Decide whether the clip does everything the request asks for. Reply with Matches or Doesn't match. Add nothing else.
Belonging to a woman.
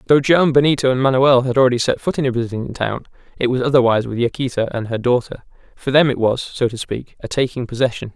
Doesn't match